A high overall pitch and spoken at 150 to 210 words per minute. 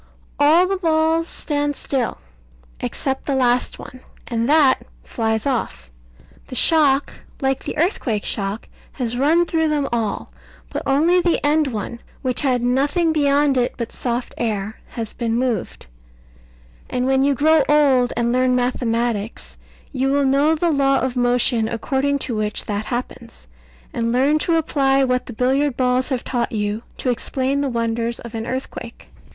Yes: very high, 260 Hz; average, 160 wpm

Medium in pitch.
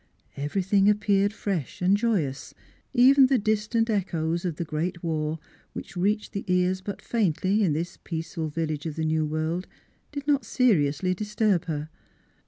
Yes: medium, 180 Hz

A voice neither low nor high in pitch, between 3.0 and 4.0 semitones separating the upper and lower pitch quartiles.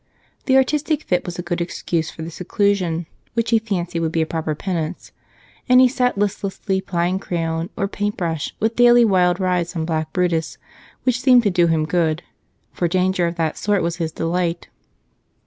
Yes: medium, 180 Hz; average, 3.5 semitones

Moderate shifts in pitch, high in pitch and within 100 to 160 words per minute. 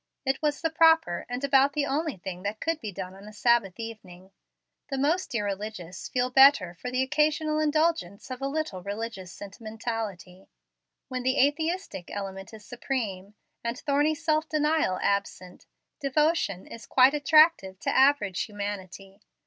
No: wide, 6.9 semitones; high, 240 Hz; average, 150 wpm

